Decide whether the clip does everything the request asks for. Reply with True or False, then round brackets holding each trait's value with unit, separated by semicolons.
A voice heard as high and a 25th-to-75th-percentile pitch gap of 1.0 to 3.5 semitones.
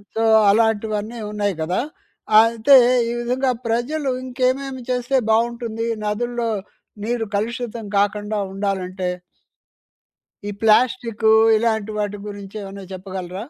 True (220 Hz; 2.8 semitones)